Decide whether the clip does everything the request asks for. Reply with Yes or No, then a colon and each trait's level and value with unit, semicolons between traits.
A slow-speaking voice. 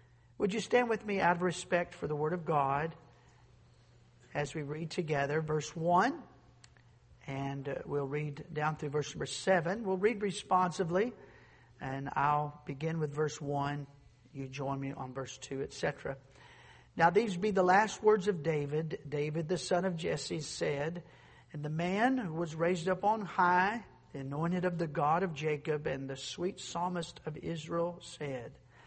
No: average, 165 wpm